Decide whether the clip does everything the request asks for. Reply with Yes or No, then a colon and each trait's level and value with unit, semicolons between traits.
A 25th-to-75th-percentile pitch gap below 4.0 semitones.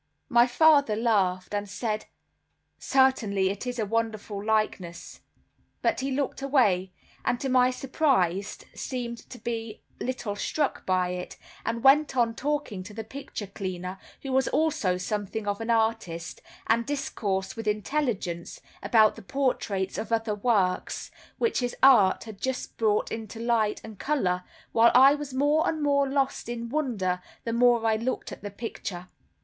No: average, 4.5 semitones